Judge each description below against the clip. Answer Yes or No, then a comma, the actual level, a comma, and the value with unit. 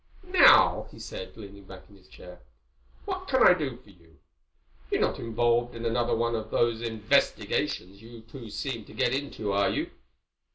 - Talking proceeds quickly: No, average, 175 wpm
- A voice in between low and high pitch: No, low, 115 Hz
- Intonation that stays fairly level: No, average, 3.6 semitones